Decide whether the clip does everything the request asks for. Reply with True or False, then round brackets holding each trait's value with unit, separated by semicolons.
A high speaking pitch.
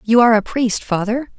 True (230 Hz)